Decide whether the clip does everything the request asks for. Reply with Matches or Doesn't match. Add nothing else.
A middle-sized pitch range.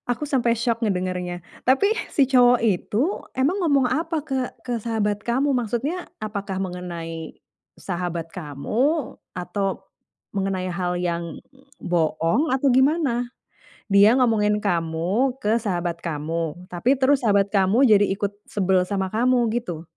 Doesn't match